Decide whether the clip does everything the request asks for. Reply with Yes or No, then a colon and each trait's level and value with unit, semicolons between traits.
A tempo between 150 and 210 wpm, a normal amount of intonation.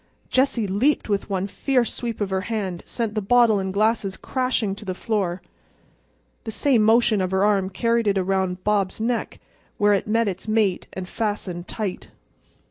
Yes: average, 180 wpm; average, 3.1 semitones